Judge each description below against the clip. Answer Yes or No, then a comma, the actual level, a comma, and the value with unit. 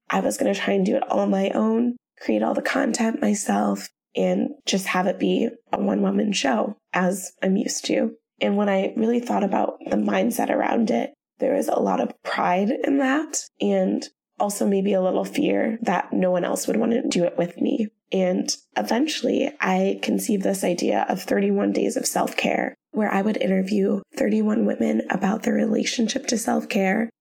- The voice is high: Yes, high, 220 Hz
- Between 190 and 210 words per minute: Yes, average, 195 wpm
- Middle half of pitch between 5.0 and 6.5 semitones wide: No, average, 4.3 semitones